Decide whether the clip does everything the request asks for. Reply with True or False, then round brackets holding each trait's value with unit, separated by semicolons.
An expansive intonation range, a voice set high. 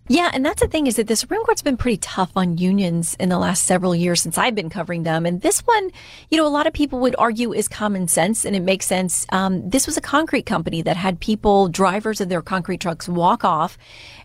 True (6.4 semitones; 195 Hz)